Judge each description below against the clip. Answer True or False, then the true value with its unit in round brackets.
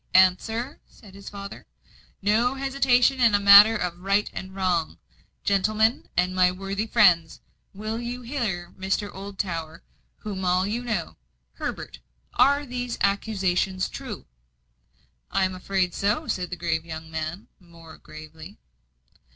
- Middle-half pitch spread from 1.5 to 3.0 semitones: False (3.7 semitones)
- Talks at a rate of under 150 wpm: True (135 wpm)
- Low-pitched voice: False (195 Hz)